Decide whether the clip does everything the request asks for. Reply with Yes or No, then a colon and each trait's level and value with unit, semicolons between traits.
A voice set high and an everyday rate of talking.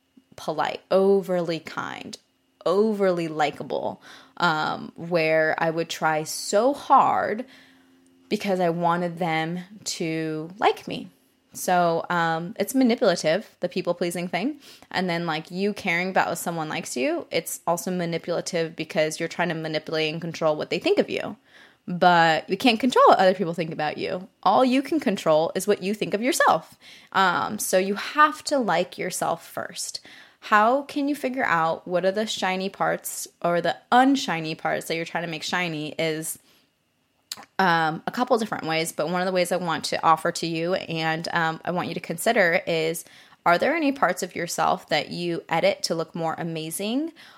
No: medium, 175 Hz; average, 175 wpm